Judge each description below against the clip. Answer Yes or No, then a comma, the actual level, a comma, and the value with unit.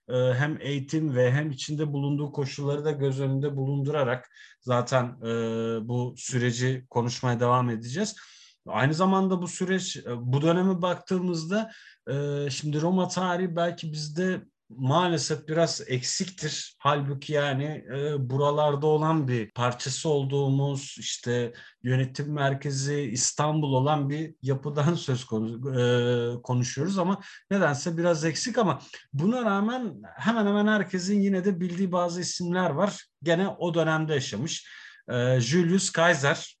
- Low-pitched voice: No, medium, 145 Hz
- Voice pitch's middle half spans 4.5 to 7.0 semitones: Yes, average, 5.2 semitones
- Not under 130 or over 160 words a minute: No, average, 120 wpm